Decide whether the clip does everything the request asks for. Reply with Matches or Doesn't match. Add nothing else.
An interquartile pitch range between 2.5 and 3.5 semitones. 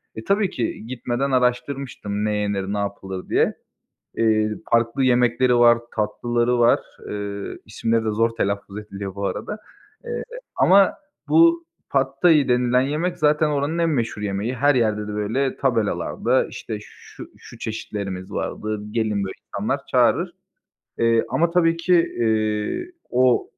Doesn't match